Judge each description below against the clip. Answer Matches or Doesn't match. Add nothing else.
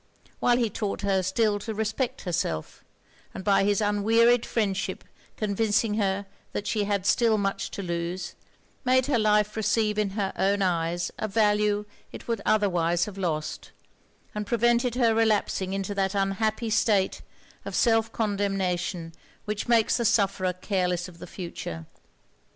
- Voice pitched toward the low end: Doesn't match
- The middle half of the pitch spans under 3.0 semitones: Matches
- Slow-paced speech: Doesn't match